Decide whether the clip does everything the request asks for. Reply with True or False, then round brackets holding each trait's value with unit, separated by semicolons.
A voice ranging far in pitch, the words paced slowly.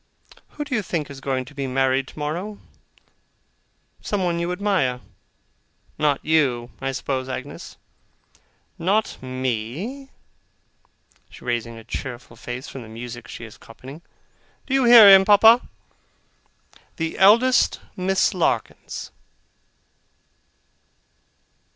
True (7.3 semitones; 110 wpm)